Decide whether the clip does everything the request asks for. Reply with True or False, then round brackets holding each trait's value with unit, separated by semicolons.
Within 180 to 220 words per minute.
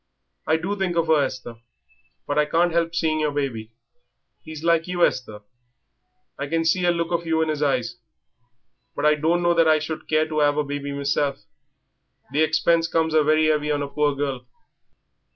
True (190 wpm)